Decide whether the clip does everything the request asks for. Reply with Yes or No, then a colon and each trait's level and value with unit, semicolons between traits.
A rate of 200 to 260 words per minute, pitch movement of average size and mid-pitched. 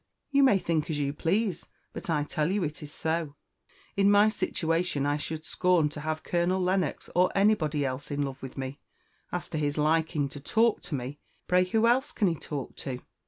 Yes: fast, 205 wpm; average, 4.0 semitones; medium, 160 Hz